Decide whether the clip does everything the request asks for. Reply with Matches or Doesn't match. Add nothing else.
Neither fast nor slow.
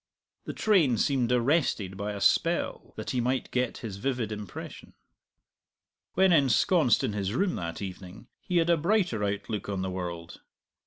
Matches